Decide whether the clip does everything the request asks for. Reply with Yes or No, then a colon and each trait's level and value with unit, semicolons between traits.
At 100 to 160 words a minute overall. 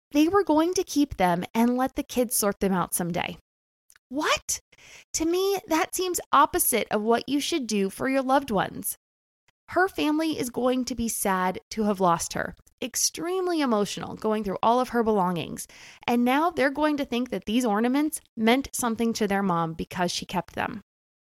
No: average, 185 wpm